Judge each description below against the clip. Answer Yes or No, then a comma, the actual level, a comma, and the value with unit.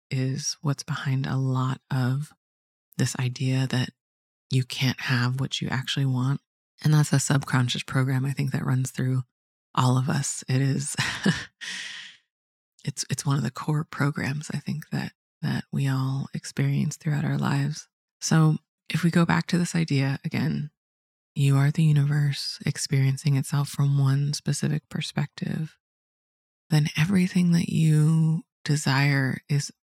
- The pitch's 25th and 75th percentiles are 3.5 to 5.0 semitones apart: No, average, 2.8 semitones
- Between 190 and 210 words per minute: No, average, 145 wpm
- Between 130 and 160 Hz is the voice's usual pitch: Yes, medium, 140 Hz